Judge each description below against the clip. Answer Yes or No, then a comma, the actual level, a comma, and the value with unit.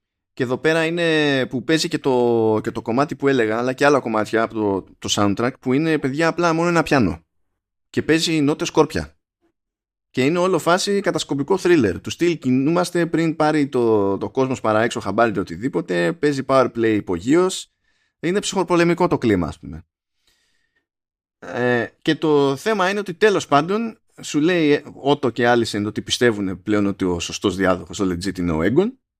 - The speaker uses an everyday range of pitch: No, wide, 7.3 semitones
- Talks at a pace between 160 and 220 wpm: Yes, fast, 170 wpm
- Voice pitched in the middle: No, low, 130 Hz